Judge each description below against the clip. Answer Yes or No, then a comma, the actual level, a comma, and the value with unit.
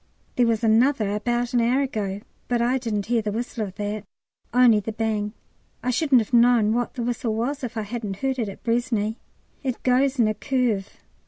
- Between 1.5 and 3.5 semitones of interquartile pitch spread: Yes, narrow, 2.6 semitones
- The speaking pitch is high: Yes, high, 235 Hz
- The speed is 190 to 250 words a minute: Yes, average, 200 wpm